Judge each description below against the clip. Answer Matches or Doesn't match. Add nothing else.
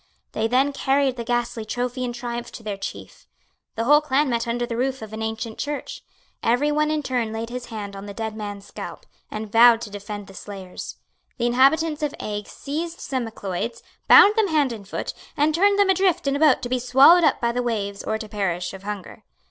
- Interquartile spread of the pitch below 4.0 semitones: Doesn't match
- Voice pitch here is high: Matches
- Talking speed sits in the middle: Doesn't match